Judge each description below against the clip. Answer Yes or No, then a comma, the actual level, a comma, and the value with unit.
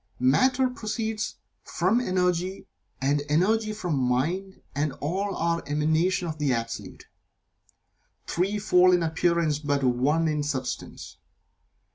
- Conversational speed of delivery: No, slow, 115 wpm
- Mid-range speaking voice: Yes, medium, 170 Hz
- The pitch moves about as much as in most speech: Yes, average, 4.7 semitones